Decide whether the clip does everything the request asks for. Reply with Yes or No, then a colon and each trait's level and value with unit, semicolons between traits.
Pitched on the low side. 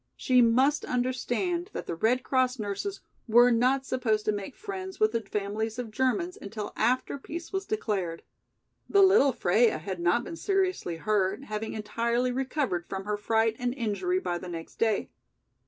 No: high, 235 Hz